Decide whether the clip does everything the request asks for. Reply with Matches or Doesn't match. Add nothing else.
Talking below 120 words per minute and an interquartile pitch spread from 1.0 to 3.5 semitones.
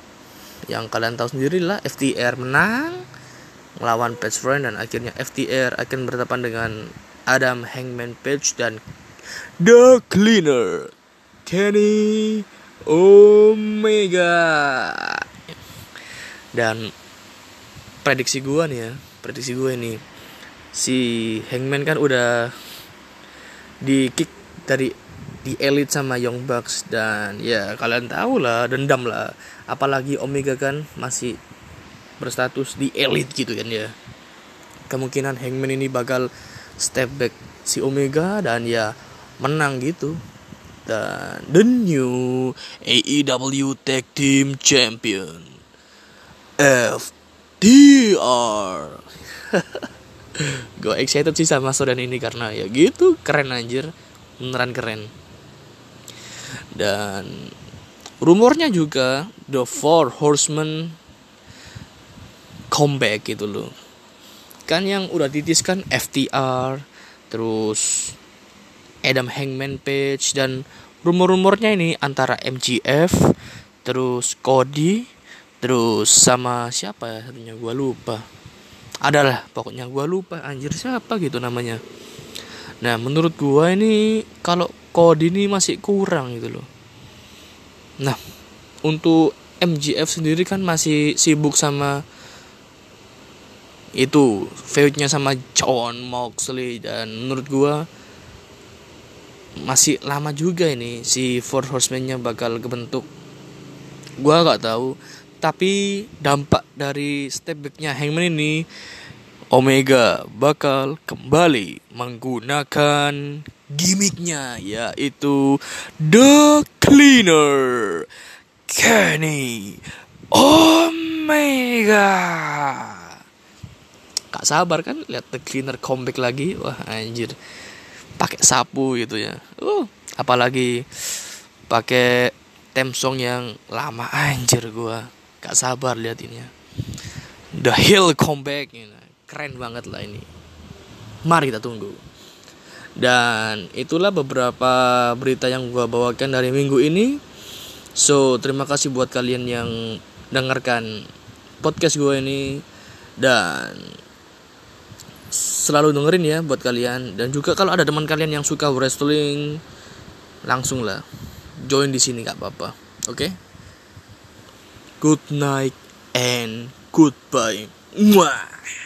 Doesn't match